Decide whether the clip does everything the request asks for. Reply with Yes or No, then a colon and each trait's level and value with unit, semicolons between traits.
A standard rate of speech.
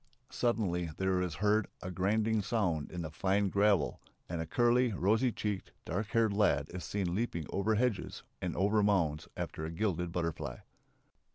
Yes: average, 165 wpm